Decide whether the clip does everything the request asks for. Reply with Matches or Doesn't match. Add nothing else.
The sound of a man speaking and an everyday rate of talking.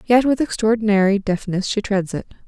Doesn't match